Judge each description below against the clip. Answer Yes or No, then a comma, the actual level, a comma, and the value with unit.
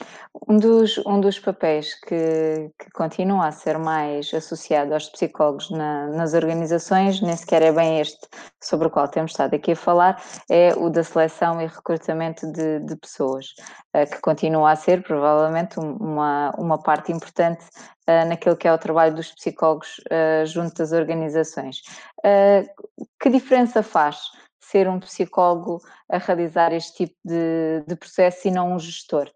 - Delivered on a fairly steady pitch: Yes, narrow, 2.2 semitones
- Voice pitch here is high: No, medium, 165 Hz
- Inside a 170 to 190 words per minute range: No, average, 155 wpm